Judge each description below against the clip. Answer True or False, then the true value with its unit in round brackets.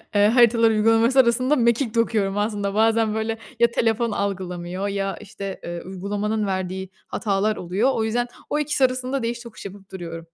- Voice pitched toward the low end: False (215 Hz)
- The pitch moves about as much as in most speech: True (3.1 semitones)